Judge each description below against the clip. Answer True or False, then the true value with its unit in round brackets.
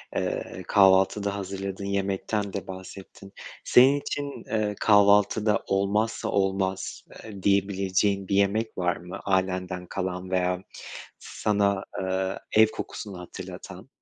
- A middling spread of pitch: False (1.5 semitones)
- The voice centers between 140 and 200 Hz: False (100 Hz)